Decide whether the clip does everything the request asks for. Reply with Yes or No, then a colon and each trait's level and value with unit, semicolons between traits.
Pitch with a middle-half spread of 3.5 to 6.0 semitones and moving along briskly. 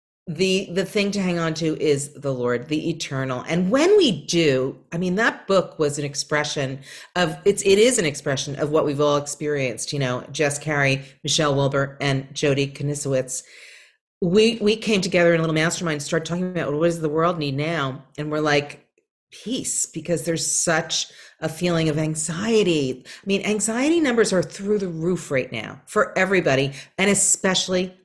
No: average, 4.3 semitones; average, 185 wpm